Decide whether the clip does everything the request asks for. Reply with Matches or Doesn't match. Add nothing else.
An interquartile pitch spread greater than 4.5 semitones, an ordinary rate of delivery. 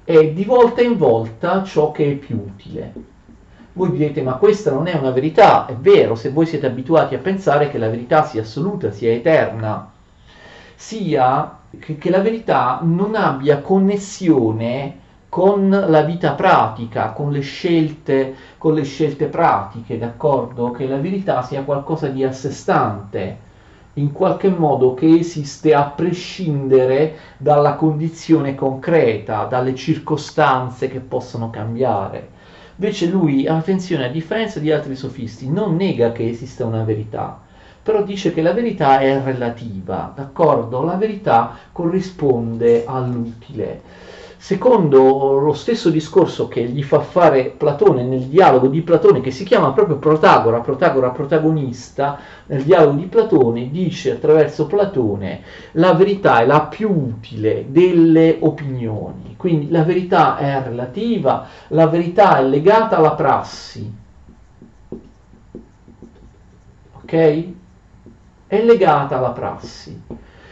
Matches